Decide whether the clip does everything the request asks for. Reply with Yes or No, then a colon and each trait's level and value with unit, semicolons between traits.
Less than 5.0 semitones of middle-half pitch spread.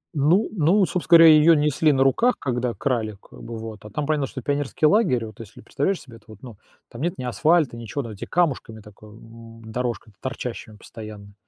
No: average, 5.3 semitones